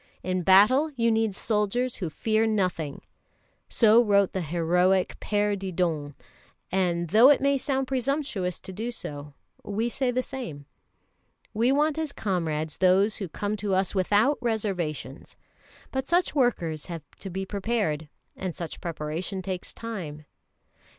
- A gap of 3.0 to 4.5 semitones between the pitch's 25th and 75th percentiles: No, average, 5.1 semitones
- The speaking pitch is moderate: No, high, 195 Hz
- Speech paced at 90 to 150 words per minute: Yes, average, 145 wpm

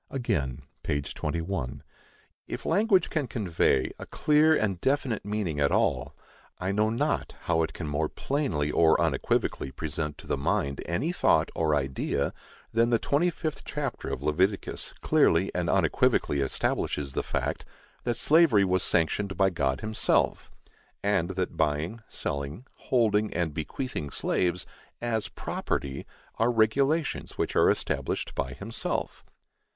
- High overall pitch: No, very low, 95 Hz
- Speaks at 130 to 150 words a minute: Yes, average, 140 wpm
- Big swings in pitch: Yes, wide, 7.9 semitones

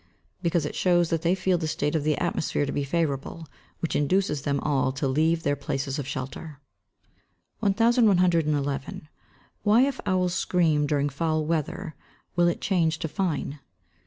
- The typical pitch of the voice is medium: Yes, medium, 160 Hz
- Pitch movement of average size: Yes, average, 3.7 semitones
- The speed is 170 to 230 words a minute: No, average, 160 wpm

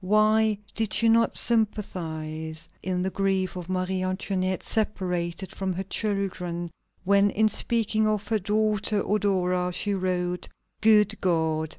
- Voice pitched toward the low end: No, high, 190 Hz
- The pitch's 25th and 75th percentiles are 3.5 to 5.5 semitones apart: No, average, 2.9 semitones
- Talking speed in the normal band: No, slow, 130 wpm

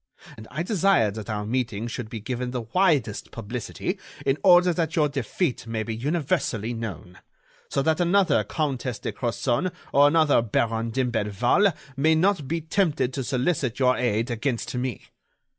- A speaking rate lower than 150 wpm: No, average, 160 wpm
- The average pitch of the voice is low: Yes, low, 130 Hz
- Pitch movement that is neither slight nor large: No, wide, 5.7 semitones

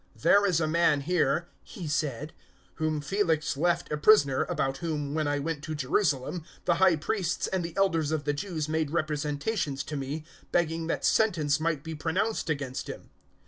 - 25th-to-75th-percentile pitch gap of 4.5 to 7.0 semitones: No, average, 2.7 semitones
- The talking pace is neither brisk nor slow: Yes, average, 185 wpm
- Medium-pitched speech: Yes, medium, 155 Hz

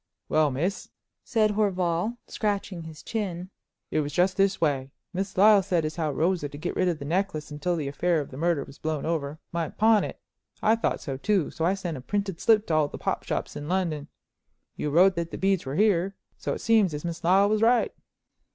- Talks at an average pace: No, fast, 220 wpm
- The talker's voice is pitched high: No, medium, 175 Hz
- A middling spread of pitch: Yes, average, 4.3 semitones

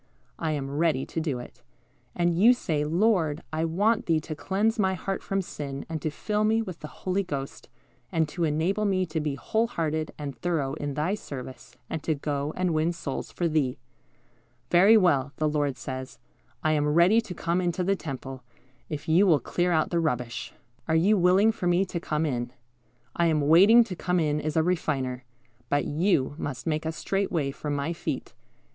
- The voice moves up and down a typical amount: Yes, average, 3.9 semitones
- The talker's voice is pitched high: No, medium, 160 Hz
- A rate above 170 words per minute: Yes, average, 200 wpm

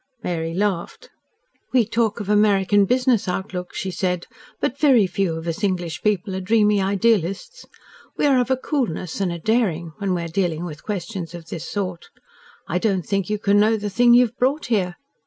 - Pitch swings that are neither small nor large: Yes, average, 4.0 semitones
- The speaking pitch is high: Yes, high, 200 Hz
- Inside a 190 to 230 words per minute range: Yes, average, 195 wpm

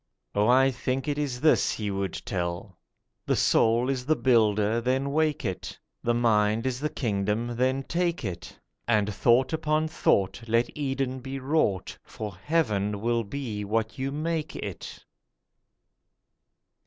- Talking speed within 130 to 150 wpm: Yes, average, 140 wpm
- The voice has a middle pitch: No, low, 120 Hz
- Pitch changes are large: No, average, 4.5 semitones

